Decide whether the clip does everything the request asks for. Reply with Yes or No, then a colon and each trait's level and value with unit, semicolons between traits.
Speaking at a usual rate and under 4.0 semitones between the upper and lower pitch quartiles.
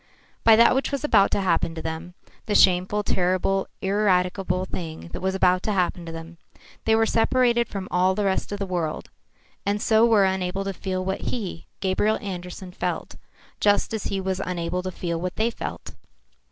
Yes: average, 185 wpm; narrow, 2.4 semitones